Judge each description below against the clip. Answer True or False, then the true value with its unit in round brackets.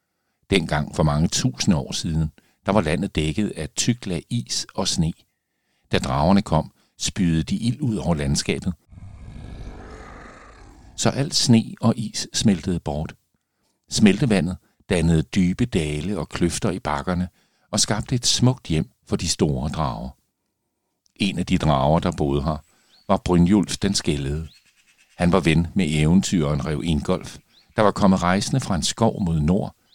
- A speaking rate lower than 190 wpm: True (150 wpm)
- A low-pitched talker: True (85 Hz)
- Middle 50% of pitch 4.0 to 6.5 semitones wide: True (4.5 semitones)